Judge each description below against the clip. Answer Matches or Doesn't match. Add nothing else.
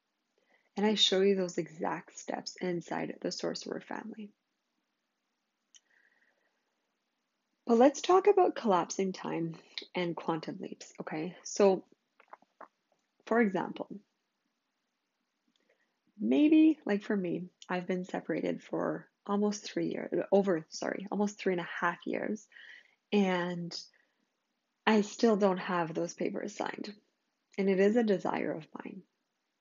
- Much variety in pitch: Matches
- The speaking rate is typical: Doesn't match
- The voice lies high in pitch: Matches